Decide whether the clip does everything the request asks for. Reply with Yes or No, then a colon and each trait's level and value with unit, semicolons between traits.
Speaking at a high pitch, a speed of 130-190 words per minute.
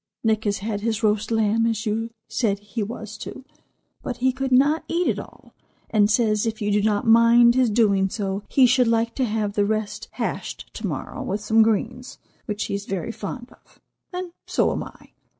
No: high, 220 Hz; fast, 205 wpm